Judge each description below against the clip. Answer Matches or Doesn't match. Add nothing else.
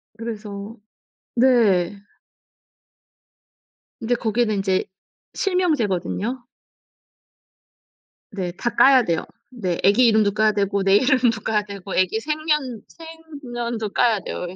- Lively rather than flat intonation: Doesn't match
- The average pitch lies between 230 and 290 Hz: Doesn't match